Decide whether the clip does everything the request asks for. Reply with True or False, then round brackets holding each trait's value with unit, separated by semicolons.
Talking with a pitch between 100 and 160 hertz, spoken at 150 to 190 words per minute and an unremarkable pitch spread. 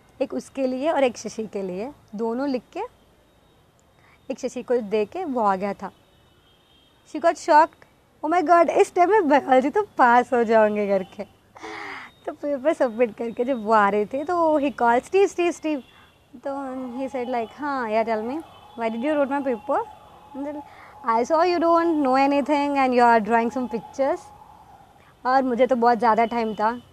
False (265 Hz; 170 wpm; 5.0 semitones)